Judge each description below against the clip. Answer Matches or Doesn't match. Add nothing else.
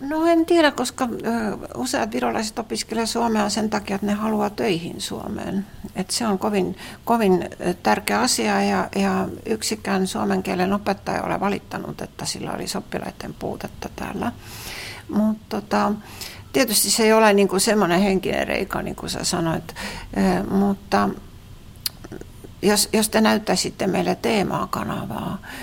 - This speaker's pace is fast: Doesn't match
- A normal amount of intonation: Doesn't match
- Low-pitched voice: Doesn't match